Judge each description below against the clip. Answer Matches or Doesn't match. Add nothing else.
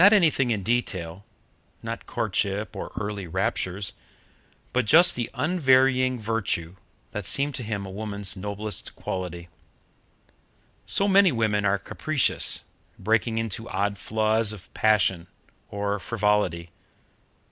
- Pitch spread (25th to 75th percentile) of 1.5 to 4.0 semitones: Matches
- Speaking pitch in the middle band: Doesn't match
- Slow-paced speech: Matches